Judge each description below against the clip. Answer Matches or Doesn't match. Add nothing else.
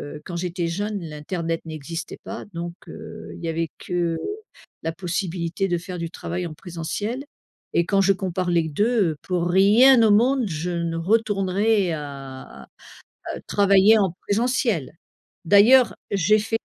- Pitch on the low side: Doesn't match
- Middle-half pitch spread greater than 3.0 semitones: Matches